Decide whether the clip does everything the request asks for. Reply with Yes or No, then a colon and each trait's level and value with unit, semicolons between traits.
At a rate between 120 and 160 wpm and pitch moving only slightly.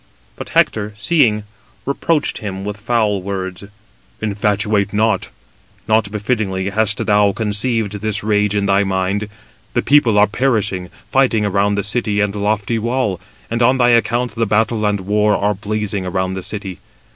Yes: average, 155 wpm; narrow, 1.9 semitones